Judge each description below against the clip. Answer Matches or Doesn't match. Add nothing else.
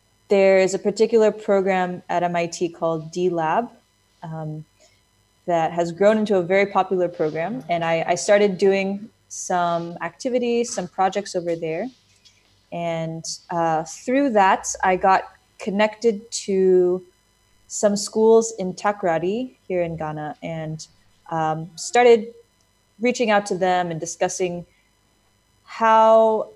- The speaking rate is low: Matches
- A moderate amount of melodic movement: Matches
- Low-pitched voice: Doesn't match